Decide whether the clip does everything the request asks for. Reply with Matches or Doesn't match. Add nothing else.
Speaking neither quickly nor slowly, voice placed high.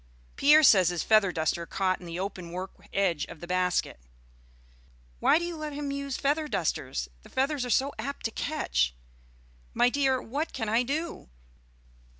Matches